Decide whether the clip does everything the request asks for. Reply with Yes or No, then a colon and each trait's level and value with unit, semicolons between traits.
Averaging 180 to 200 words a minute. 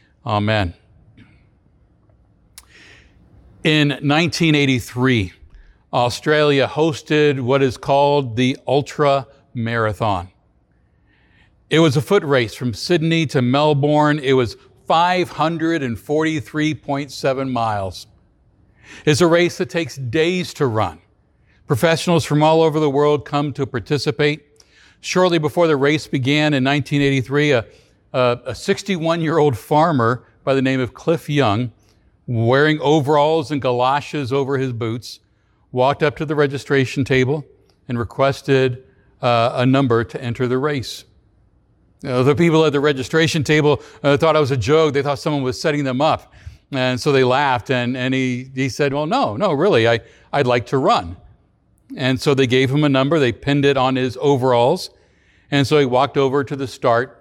No: average, 150 wpm